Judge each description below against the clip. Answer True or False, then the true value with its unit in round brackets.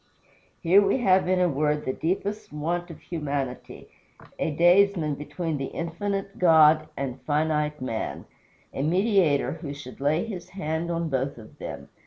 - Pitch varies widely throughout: False (3.6 semitones)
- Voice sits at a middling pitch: True (160 Hz)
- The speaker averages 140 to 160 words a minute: True (155 wpm)